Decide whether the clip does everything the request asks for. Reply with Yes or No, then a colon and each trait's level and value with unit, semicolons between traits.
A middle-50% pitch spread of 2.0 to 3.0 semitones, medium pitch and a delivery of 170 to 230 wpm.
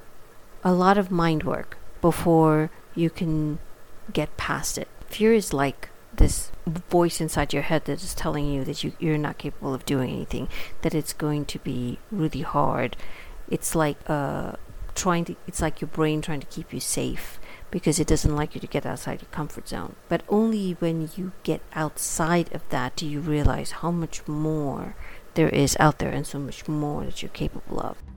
Yes: average, 2.7 semitones; medium, 155 Hz; average, 190 wpm